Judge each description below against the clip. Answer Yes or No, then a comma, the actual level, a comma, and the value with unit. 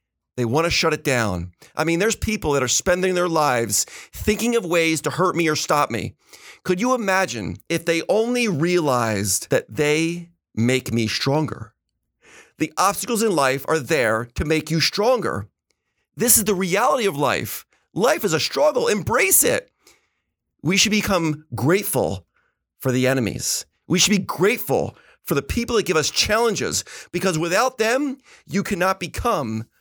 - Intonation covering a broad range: Yes, wide, 7.0 semitones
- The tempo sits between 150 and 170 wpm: Yes, average, 165 wpm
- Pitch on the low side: No, medium, 160 Hz